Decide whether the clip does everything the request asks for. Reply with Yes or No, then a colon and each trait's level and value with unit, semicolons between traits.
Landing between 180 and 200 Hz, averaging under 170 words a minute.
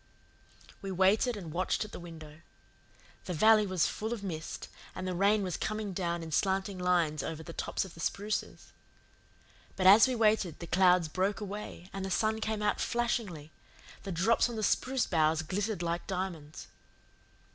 No: high, 190 Hz; average, 175 wpm